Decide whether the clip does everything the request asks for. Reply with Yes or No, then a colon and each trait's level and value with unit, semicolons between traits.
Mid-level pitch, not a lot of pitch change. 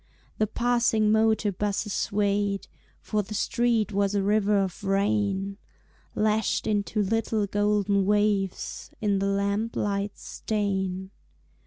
No: high, 205 Hz; narrow, 1.3 semitones